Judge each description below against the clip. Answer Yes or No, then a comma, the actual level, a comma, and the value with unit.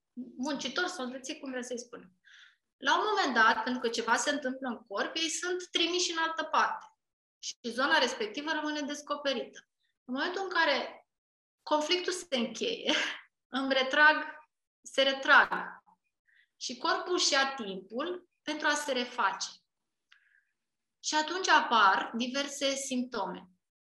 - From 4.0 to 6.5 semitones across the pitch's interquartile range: Yes, average, 4.7 semitones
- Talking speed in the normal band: Yes, average, 130 wpm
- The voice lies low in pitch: No, very high, 290 Hz